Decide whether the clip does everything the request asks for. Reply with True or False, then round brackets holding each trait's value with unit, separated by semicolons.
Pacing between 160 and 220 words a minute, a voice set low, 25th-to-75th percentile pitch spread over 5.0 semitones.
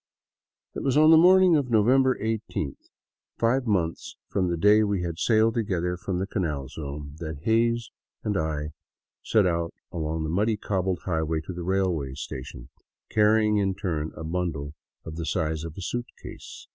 True (170 wpm; 90 Hz; 5.6 semitones)